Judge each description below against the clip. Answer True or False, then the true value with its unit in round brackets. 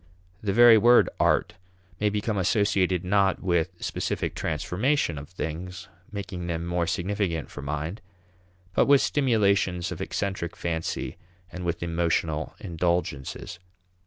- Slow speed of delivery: True (125 wpm)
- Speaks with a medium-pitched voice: False (90 Hz)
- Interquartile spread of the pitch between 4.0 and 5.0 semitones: False (3.3 semitones)